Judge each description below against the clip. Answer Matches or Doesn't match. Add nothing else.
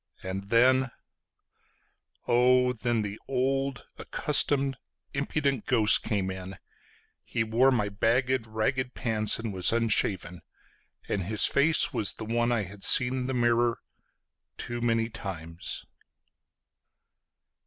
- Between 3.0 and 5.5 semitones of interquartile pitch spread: Matches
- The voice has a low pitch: Matches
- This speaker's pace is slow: Matches